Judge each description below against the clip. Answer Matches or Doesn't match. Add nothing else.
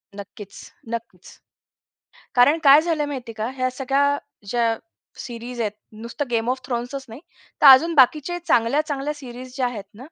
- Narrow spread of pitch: Doesn't match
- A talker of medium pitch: Doesn't match